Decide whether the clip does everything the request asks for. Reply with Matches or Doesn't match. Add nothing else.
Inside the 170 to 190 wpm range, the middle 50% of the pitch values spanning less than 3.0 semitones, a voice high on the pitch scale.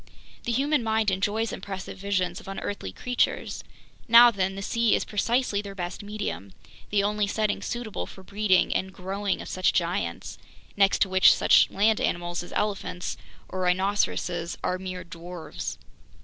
Doesn't match